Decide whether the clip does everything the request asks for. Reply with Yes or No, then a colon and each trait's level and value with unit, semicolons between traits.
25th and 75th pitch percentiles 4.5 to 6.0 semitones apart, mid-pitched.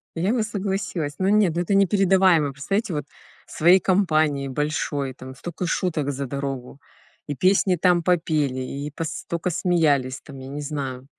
Yes: average, 4.8 semitones; medium, 155 Hz